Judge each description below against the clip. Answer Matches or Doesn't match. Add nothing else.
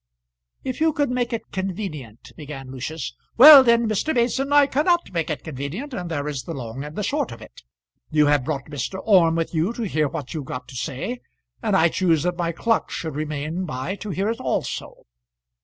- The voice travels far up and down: Matches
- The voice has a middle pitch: Matches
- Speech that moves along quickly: Matches